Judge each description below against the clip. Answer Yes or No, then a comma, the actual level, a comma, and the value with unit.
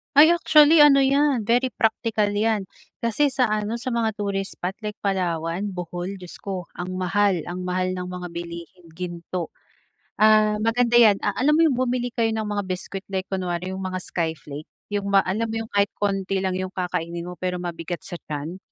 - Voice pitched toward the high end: Yes, high, 195 Hz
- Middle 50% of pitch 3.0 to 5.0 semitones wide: Yes, average, 3.8 semitones